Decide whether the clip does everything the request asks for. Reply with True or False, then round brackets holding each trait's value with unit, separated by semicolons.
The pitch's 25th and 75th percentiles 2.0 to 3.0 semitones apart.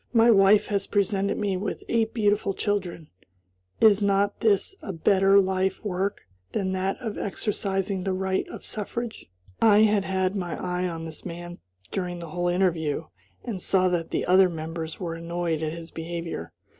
True (2.7 semitones)